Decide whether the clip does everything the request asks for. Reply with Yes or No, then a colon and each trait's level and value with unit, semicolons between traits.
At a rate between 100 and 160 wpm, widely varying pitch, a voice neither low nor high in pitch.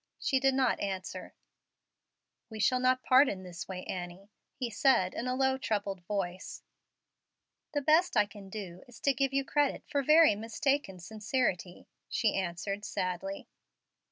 No: average, 155 wpm; wide, 5.8 semitones; high, 215 Hz